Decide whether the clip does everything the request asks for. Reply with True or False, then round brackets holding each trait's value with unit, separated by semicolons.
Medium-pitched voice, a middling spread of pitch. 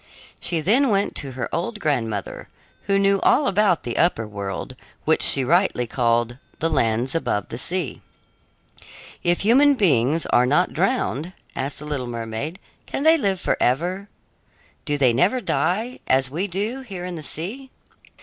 False (165 Hz; 7.7 semitones)